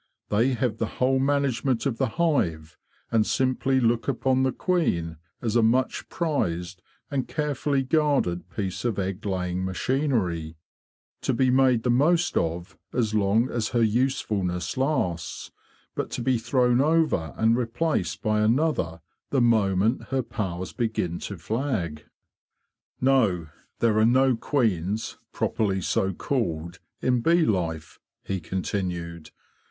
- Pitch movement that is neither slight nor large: No, wide, 6.1 semitones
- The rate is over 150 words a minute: No, average, 140 wpm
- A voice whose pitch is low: Yes, low, 115 Hz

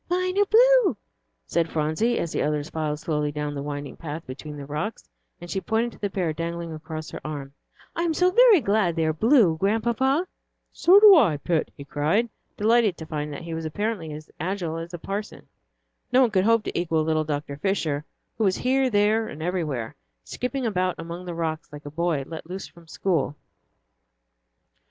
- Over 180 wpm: Yes, average, 195 wpm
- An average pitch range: No, wide, 6.3 semitones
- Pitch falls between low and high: Yes, medium, 170 Hz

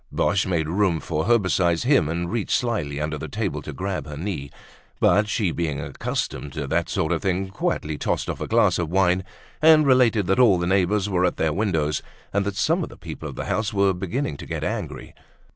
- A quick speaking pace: Yes, fast, 220 wpm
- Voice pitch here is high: No, very low, 95 Hz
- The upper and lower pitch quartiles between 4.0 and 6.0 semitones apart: Yes, average, 4.4 semitones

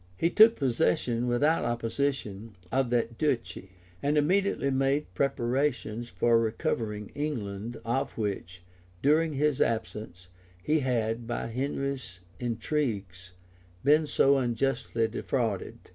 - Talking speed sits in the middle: No, slow, 115 wpm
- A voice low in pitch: Yes, low, 120 Hz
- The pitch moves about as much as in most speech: Yes, average, 3.9 semitones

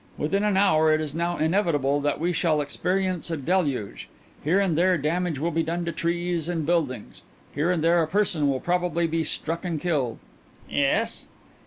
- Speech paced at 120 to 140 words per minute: No, average, 185 wpm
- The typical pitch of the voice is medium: Yes, medium, 165 Hz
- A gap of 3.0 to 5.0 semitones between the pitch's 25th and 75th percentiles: No, narrow, 2.6 semitones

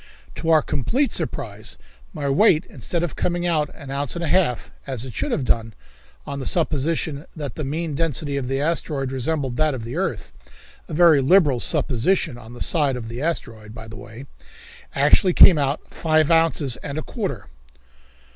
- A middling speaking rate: Yes, average, 185 wpm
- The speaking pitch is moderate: Yes, medium, 145 Hz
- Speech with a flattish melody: No, average, 4.2 semitones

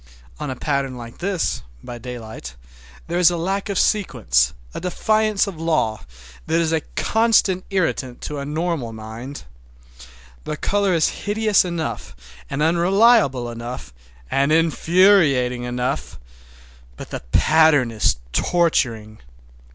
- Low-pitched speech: No, medium, 155 Hz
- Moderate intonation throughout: No, wide, 6.7 semitones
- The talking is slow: Yes, slow, 130 wpm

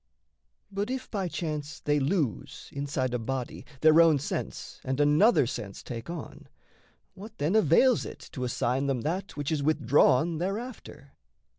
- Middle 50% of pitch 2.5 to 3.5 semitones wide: No, wide, 5.4 semitones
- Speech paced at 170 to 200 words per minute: No, average, 150 wpm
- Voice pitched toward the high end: No, medium, 150 Hz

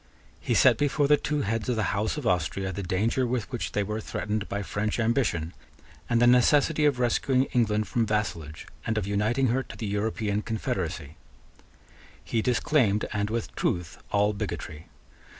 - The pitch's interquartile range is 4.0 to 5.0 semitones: No, average, 3.3 semitones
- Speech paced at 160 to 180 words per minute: Yes, average, 170 wpm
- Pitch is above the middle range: No, low, 110 Hz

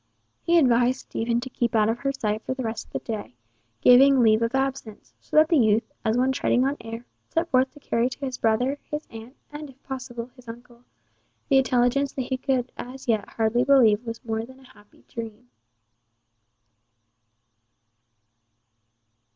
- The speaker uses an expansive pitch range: No, average, 2.7 semitones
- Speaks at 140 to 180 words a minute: Yes, average, 175 wpm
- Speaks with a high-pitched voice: Yes, high, 245 Hz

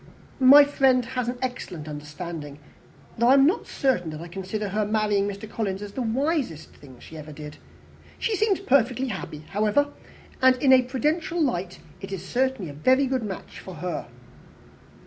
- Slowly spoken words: No, average, 175 wpm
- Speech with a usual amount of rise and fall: No, wide, 6.8 semitones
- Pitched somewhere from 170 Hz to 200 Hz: No, high, 220 Hz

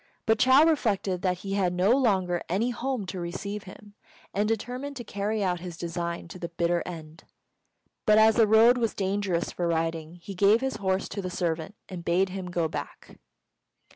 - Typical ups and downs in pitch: Yes, average, 3.9 semitones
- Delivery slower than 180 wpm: No, average, 190 wpm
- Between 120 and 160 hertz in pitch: No, high, 190 Hz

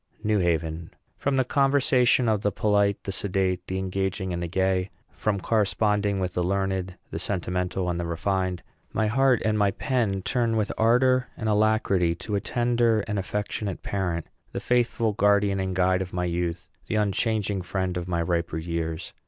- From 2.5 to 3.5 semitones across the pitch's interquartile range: Yes, average, 3.2 semitones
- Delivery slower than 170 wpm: No, average, 175 wpm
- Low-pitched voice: Yes, low, 100 Hz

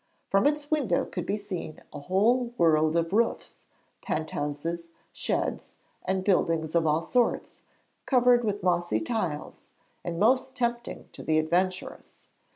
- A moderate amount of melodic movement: No, wide, 6.3 semitones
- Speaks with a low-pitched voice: No, medium, 185 Hz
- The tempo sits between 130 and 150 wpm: Yes, slow, 135 wpm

